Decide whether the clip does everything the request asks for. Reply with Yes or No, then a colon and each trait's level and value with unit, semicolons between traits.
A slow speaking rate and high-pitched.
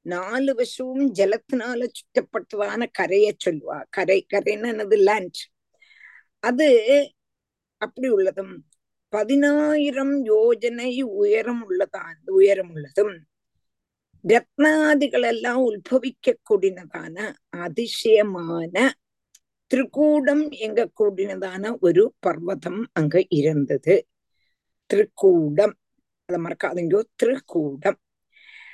Yes: slow, 65 wpm; high, 230 Hz